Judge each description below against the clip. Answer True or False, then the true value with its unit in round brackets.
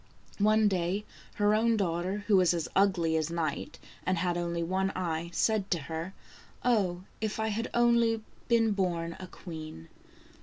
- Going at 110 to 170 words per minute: True (165 wpm)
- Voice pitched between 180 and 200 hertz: True (185 Hz)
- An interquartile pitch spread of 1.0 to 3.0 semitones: False (4.0 semitones)